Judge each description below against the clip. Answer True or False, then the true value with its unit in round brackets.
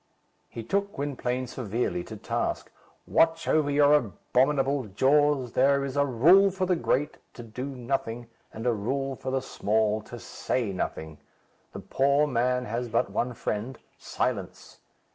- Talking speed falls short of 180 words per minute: True (150 wpm)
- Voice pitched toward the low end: True (130 Hz)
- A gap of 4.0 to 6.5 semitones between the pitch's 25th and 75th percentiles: False (3.5 semitones)